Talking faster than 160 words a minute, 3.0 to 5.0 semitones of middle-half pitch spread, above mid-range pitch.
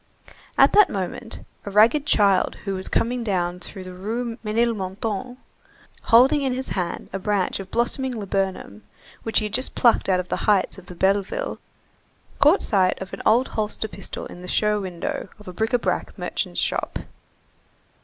Yes: average, 170 wpm; average, 3.8 semitones; high, 210 Hz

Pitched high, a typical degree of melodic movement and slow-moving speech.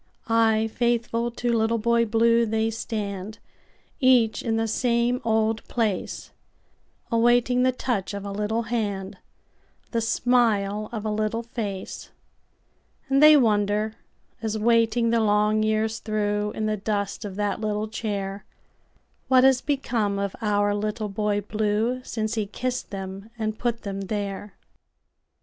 No: high, 220 Hz; narrow, 2.0 semitones; slow, 125 wpm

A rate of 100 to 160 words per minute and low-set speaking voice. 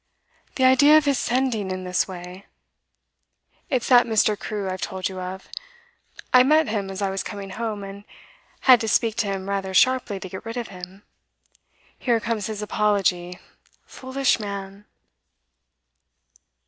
No: average, 155 wpm; high, 205 Hz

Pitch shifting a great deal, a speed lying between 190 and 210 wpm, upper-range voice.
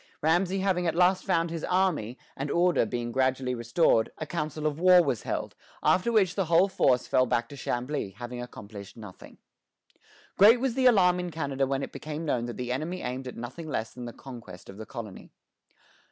No: wide, 6.6 semitones; average, 195 wpm; medium, 145 Hz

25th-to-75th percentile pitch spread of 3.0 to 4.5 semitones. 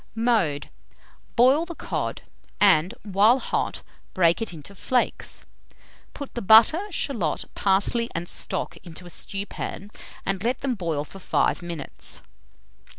No: wide, 5.6 semitones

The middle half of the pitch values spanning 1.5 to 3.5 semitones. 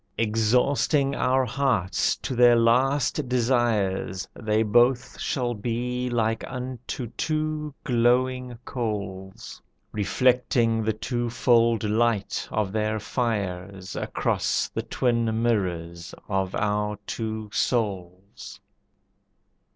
Yes: average, 3.1 semitones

